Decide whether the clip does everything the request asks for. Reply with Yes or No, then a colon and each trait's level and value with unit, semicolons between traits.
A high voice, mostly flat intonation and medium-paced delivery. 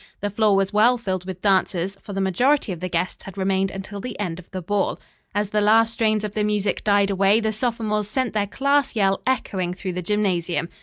No: high, 205 Hz; narrow, 2.2 semitones; fast, 220 wpm